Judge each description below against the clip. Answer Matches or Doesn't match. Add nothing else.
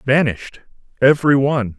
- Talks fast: Doesn't match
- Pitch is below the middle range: Matches